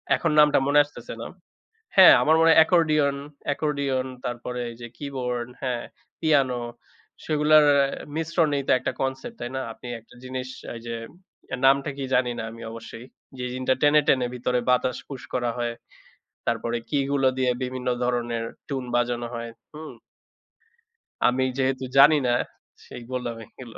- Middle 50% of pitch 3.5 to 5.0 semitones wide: No, average, 3.1 semitones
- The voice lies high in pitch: No, low, 130 Hz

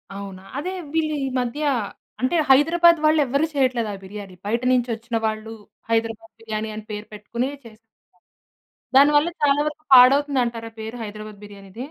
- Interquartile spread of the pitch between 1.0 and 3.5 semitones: No, average, 4.6 semitones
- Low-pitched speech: No, high, 235 Hz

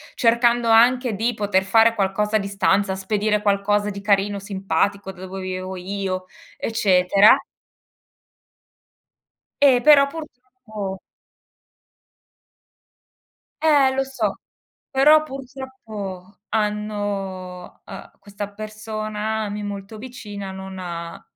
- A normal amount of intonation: Yes, average, 3.1 semitones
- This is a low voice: No, high, 205 Hz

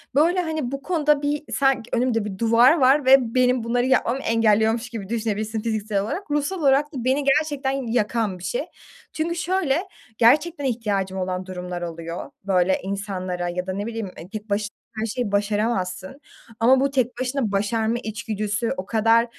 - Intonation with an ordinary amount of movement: Yes, average, 4.9 semitones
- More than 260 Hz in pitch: No, high, 230 Hz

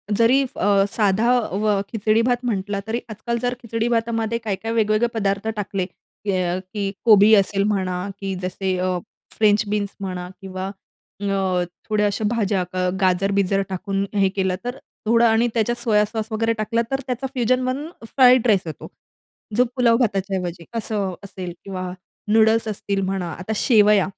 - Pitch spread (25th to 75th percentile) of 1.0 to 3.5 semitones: Yes, average, 2.8 semitones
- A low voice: No, high, 210 Hz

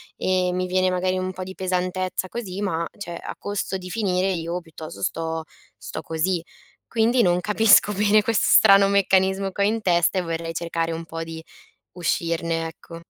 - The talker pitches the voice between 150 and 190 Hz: Yes, medium, 185 Hz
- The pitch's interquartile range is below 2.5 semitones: No, average, 2.8 semitones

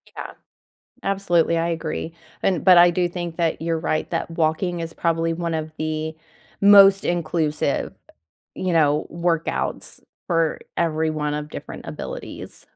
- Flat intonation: Yes, narrow, 1.8 semitones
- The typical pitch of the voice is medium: Yes, medium, 165 Hz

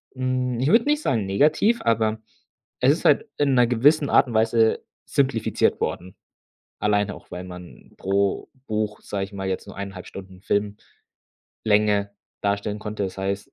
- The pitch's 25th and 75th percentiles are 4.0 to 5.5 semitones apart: Yes, average, 4.3 semitones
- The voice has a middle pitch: No, low, 105 Hz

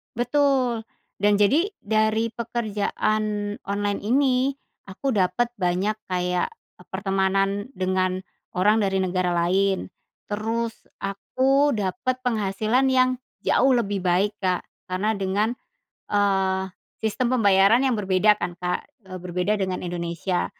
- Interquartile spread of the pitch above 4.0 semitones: No, average, 3.6 semitones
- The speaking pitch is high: Yes, high, 205 Hz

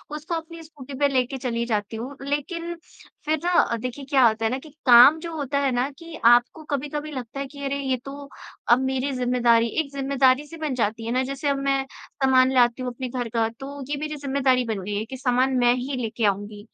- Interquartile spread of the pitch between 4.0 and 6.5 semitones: No, average, 2.8 semitones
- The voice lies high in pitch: Yes, very high, 265 Hz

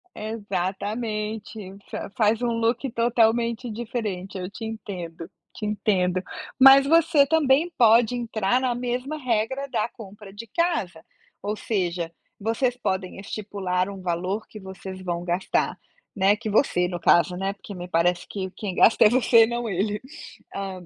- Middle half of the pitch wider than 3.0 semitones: Yes, average, 3.9 semitones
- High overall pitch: Yes, high, 210 Hz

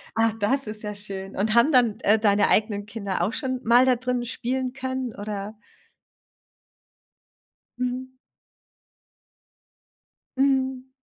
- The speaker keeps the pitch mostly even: No, average, 3.7 semitones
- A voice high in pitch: Yes, high, 235 Hz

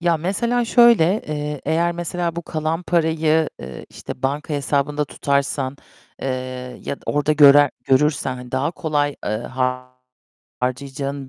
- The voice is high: No, medium, 145 Hz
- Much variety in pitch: No, average, 3.1 semitones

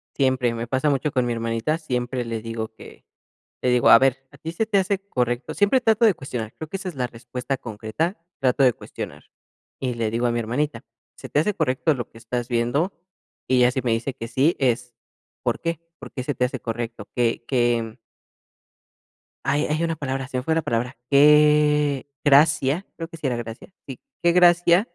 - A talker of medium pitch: No, low, 130 Hz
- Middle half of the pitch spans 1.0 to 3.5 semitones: No, average, 4.3 semitones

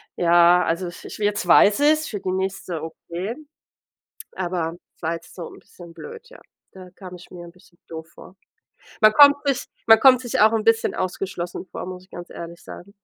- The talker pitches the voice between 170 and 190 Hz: Yes, medium, 185 Hz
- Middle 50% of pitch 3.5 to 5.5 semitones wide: Yes, average, 3.9 semitones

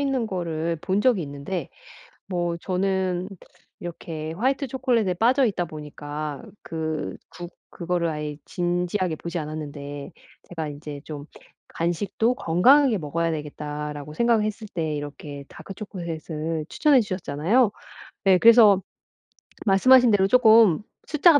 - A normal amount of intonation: No, wide, 5.7 semitones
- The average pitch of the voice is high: No, medium, 175 Hz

